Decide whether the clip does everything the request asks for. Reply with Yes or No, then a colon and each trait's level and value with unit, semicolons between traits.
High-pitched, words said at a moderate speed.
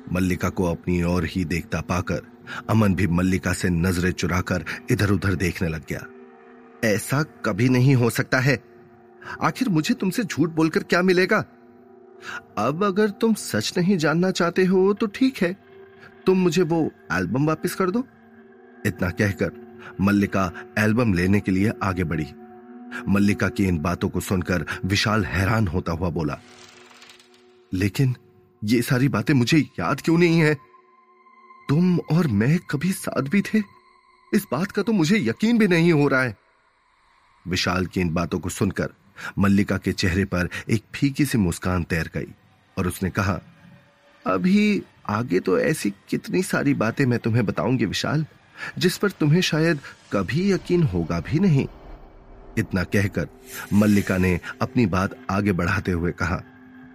No: low, 120 Hz; average, 150 wpm